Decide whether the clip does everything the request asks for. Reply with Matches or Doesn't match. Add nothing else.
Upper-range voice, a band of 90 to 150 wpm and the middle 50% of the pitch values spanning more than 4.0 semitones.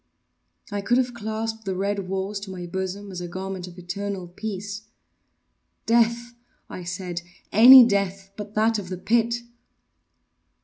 Doesn't match